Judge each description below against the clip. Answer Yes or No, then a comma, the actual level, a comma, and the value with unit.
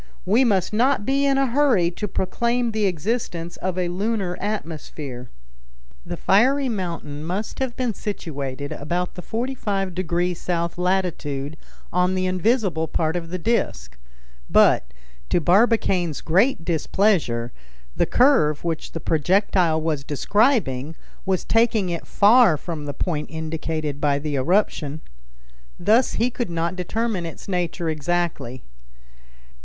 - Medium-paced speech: No, slow, 130 wpm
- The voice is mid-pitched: Yes, medium, 180 Hz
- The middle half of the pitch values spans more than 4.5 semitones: Yes, average, 5.2 semitones